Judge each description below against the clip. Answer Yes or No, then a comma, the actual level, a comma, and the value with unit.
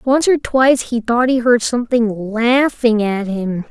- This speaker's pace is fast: No, average, 180 wpm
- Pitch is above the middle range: Yes, high, 235 Hz